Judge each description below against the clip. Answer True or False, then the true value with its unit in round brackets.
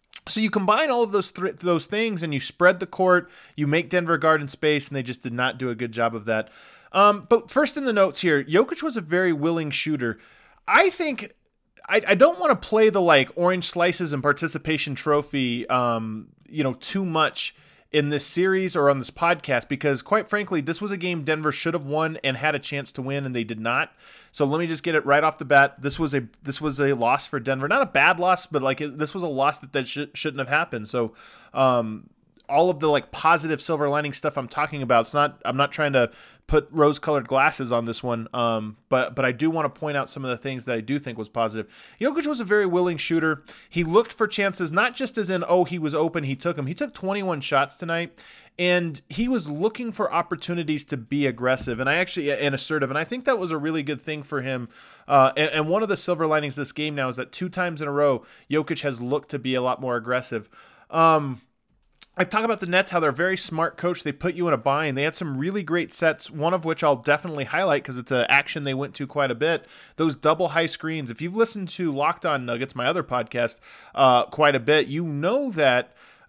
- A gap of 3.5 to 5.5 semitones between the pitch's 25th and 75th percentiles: True (4.5 semitones)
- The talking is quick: True (245 wpm)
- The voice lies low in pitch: False (155 Hz)